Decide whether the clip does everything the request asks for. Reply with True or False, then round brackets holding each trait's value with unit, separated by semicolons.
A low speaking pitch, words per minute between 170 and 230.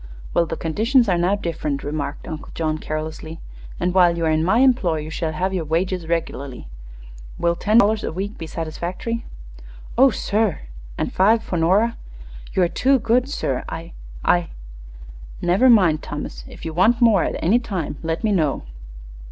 False (175 Hz; 175 wpm)